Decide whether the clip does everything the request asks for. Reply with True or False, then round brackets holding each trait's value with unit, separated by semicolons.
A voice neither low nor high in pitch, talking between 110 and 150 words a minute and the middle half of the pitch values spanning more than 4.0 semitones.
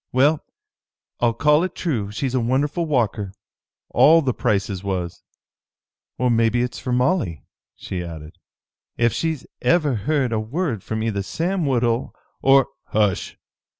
False (125 Hz; 145 wpm; 5.6 semitones)